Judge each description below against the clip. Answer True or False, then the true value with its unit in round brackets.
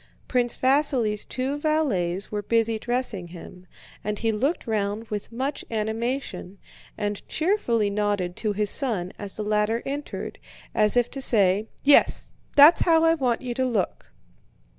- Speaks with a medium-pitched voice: False (225 Hz)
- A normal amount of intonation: True (4.2 semitones)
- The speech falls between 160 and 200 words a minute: False (150 wpm)